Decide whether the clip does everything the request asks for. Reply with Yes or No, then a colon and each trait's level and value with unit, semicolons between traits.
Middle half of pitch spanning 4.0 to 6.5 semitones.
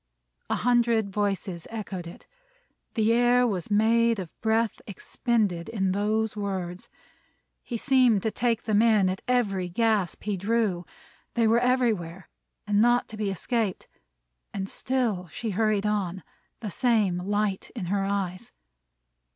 No: average, 3.3 semitones